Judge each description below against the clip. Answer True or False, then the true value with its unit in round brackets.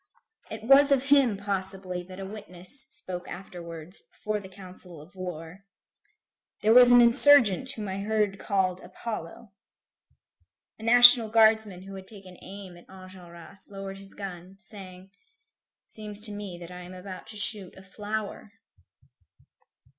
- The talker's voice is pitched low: False (195 Hz)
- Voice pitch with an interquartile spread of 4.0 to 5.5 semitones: False (2.9 semitones)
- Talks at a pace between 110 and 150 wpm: True (145 wpm)